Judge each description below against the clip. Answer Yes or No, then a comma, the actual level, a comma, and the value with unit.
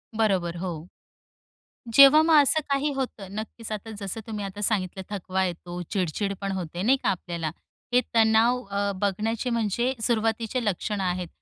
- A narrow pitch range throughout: No, average, 3.6 semitones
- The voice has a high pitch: Yes, high, 205 Hz